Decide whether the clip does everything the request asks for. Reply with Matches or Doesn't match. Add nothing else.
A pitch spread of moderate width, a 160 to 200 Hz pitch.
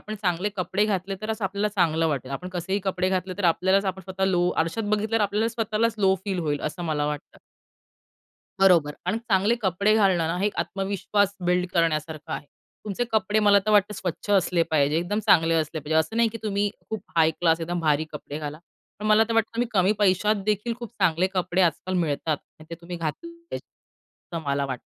Matches